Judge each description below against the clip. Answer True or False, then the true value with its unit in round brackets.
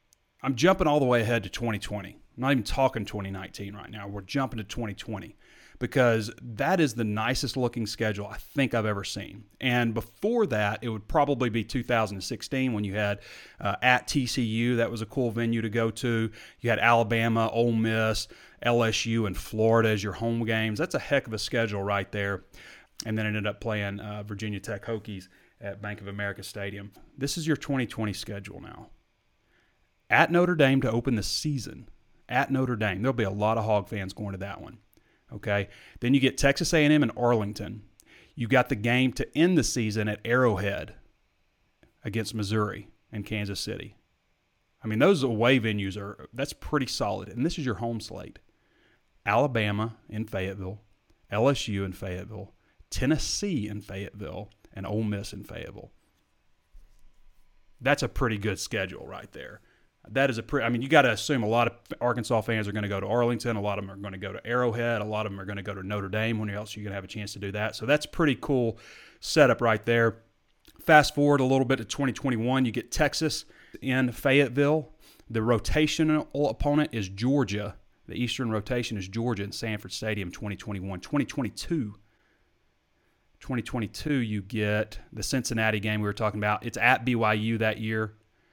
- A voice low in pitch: True (110 Hz)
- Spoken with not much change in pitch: False (3.3 semitones)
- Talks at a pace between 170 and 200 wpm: True (185 wpm)